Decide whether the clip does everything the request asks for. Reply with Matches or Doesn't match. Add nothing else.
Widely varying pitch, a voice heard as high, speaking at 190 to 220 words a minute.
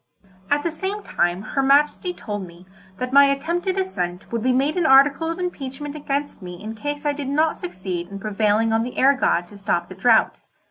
Matches